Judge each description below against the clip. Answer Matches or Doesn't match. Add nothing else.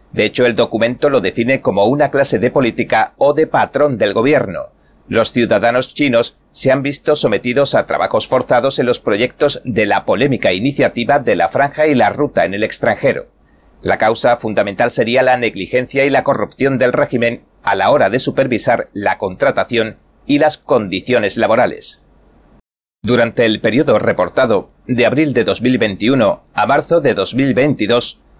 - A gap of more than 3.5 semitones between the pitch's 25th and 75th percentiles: Doesn't match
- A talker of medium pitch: Doesn't match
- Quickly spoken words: Doesn't match